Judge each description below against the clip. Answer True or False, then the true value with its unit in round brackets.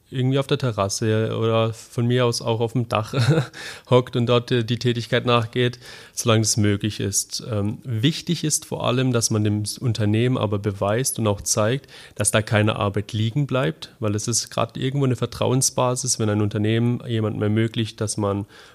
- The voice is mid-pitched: False (115 Hz)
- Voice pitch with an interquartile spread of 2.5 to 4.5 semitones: True (2.8 semitones)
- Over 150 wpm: True (180 wpm)